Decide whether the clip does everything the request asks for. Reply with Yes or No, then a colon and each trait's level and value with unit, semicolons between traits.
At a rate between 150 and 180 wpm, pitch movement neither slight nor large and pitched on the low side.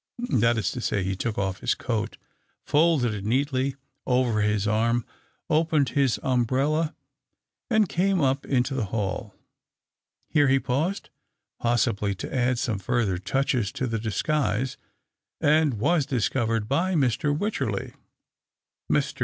No: slow, 135 wpm; average, 4.9 semitones; low, 125 Hz